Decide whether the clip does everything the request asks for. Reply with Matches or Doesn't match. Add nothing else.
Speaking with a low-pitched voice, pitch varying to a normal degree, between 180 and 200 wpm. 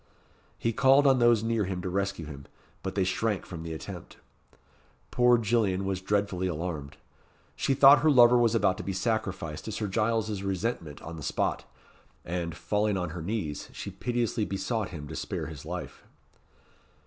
Doesn't match